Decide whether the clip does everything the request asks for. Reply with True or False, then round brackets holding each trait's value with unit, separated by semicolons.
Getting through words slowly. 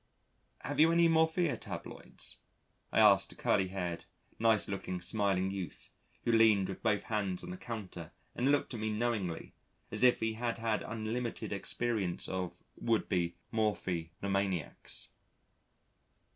False (145 wpm)